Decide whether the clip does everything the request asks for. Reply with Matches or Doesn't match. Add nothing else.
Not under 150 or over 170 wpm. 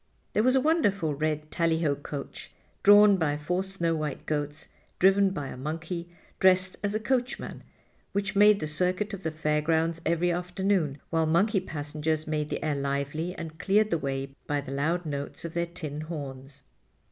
Doesn't match